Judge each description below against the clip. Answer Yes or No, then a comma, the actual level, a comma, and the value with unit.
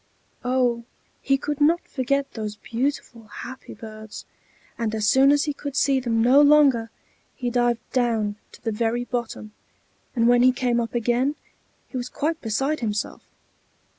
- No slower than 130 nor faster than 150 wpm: No, average, 160 wpm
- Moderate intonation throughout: Yes, average, 3.2 semitones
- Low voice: No, high, 245 Hz